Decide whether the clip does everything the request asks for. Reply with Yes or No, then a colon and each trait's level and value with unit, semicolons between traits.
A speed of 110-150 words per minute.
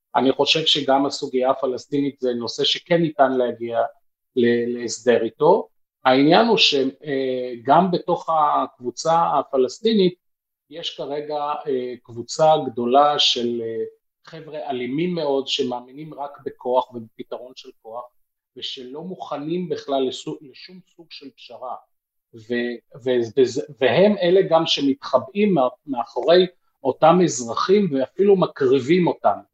No: slow, 100 wpm